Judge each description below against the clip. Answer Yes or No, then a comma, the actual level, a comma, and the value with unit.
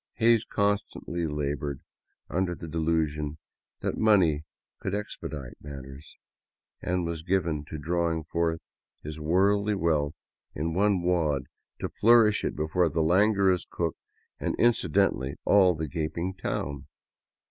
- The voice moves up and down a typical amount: Yes, average, 3.9 semitones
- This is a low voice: Yes, very low, 85 Hz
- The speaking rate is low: Yes, slow, 125 wpm